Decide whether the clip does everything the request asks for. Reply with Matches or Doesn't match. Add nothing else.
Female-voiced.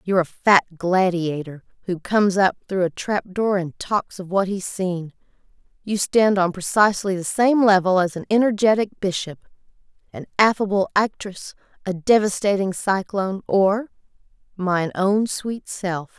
Matches